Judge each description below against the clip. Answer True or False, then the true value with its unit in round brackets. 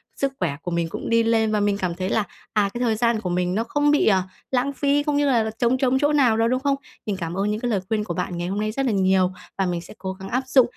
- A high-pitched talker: True (220 Hz)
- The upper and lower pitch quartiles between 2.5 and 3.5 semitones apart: False (5.1 semitones)